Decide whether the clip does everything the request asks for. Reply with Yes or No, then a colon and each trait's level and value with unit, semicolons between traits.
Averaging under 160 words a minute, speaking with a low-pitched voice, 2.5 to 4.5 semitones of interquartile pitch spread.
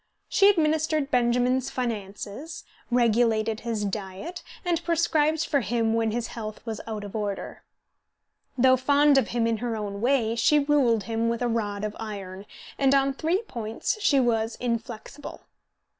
No: average, 150 wpm; high, 235 Hz; average, 4.2 semitones